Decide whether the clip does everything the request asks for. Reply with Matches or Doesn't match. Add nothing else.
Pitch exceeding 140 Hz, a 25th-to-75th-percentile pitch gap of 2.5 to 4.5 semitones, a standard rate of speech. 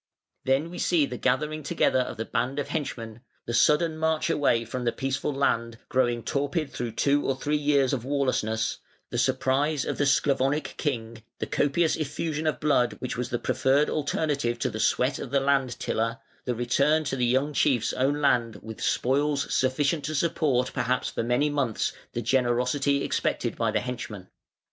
Doesn't match